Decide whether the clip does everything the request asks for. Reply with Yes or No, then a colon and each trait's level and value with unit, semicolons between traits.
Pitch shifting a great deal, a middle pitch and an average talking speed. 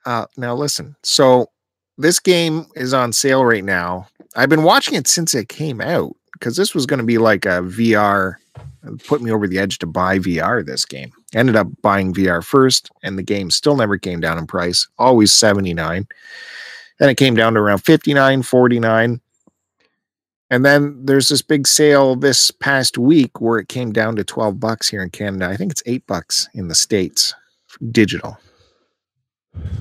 No: wide, 5.9 semitones; low, 115 Hz; average, 185 wpm